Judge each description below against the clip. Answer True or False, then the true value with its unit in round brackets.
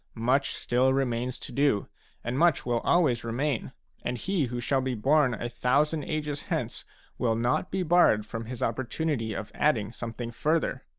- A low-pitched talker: True (125 Hz)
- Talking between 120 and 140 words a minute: False (170 wpm)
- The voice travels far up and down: False (4.2 semitones)